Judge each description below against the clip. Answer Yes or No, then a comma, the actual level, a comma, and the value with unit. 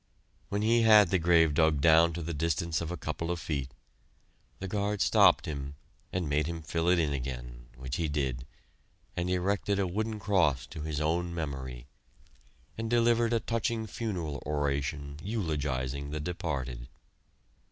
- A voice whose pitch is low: Yes, very low, 80 Hz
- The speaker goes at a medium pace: Yes, average, 160 wpm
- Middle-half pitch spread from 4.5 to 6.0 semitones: Yes, average, 4.9 semitones